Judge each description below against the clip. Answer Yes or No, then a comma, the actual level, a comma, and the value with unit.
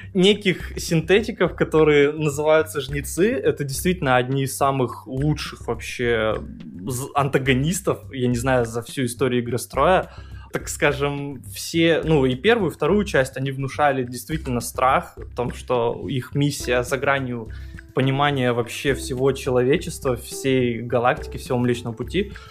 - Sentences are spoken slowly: No, average, 135 wpm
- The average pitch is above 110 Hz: Yes, low, 135 Hz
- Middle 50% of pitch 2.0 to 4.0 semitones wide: Yes, average, 3.4 semitones